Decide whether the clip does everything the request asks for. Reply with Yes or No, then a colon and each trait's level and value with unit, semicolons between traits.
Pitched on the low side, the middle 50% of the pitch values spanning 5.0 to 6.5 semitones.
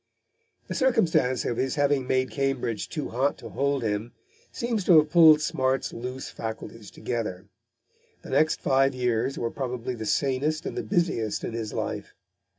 No: low, 130 Hz; average, 4.2 semitones